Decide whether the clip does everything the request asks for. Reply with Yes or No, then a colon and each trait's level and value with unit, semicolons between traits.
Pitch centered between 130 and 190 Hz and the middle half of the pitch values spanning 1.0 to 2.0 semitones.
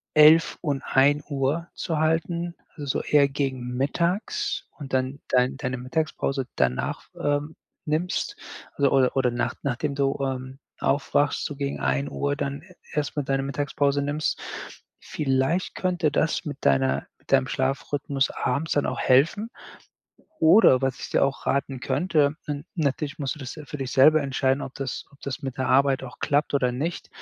No: medium, 140 Hz; narrow, 2.4 semitones